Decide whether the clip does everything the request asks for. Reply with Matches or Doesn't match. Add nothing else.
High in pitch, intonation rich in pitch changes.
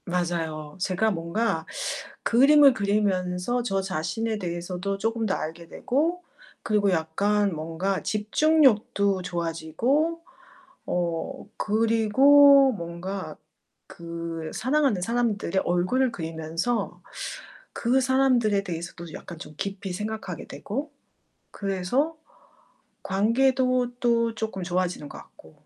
Matches